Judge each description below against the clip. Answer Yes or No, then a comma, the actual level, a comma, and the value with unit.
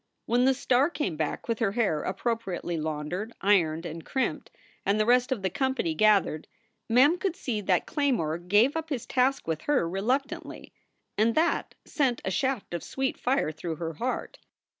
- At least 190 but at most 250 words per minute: No, average, 175 wpm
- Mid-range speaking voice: No, high, 225 Hz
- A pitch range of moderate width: No, wide, 7.3 semitones